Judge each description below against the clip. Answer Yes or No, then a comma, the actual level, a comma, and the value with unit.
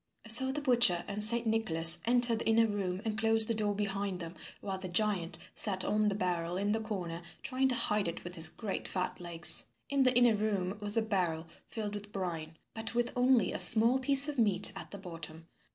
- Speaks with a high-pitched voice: Yes, high, 210 Hz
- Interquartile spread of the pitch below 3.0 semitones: No, average, 4.0 semitones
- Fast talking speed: Yes, fast, 215 wpm